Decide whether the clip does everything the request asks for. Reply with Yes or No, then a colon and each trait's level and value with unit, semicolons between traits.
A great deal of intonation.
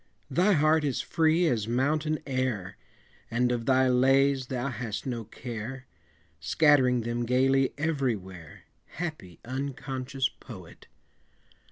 No: average, 3.0 semitones